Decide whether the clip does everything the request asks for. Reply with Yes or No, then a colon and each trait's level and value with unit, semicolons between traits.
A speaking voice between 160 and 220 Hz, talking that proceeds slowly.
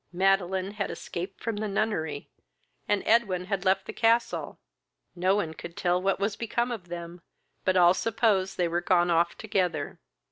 No: high, 190 Hz; average, 170 wpm